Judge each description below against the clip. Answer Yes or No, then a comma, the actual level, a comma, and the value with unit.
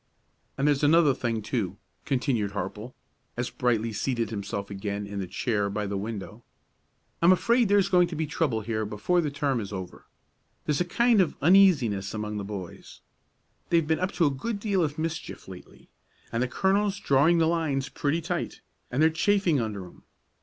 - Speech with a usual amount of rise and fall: No, wide, 8.1 semitones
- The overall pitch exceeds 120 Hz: Yes, low, 135 Hz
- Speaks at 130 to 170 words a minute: No, average, 180 wpm